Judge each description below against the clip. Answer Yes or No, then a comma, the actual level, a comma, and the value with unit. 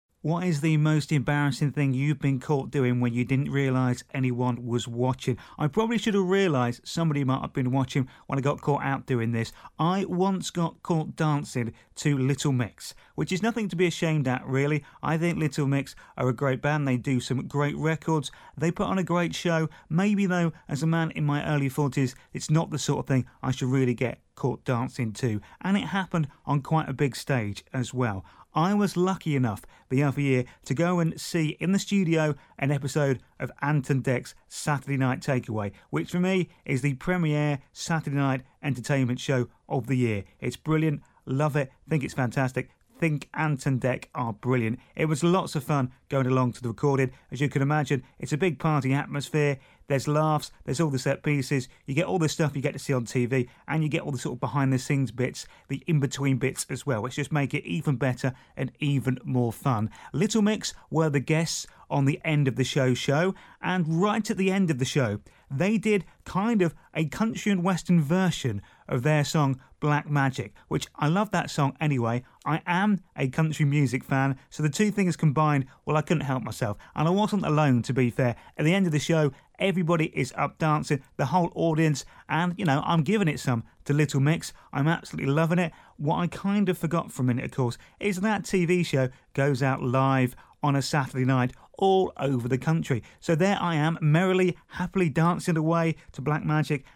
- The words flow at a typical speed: No, fast, 210 wpm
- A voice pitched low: No, medium, 145 Hz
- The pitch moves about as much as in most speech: Yes, average, 3.9 semitones